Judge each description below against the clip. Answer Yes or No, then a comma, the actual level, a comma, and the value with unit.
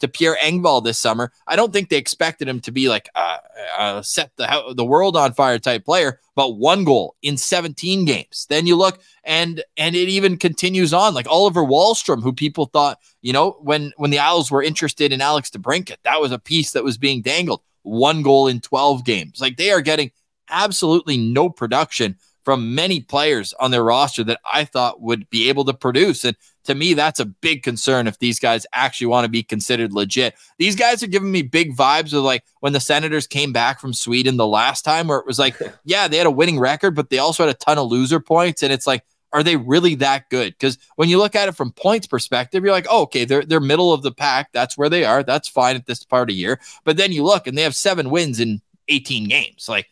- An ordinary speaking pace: No, fast, 235 wpm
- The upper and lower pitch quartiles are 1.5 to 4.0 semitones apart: No, average, 4.5 semitones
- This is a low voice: No, medium, 145 Hz